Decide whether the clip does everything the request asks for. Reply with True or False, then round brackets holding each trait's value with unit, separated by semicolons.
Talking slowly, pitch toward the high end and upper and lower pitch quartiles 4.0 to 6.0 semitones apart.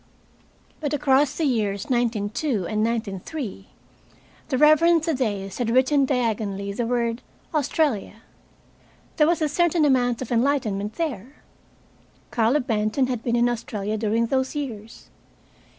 True (125 wpm; 240 Hz; 4.8 semitones)